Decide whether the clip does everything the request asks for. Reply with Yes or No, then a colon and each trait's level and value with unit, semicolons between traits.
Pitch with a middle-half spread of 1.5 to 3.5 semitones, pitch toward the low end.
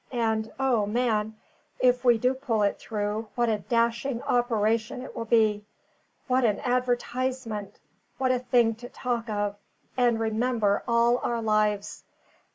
No: narrow, 2.4 semitones; high, 230 Hz